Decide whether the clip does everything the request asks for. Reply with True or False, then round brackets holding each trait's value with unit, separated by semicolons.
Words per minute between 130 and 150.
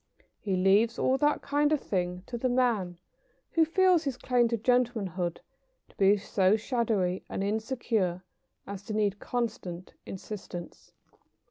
True (140 wpm)